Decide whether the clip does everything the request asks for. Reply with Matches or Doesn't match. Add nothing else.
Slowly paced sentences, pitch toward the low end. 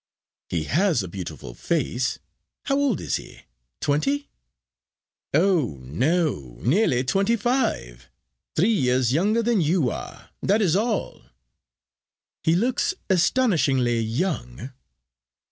Doesn't match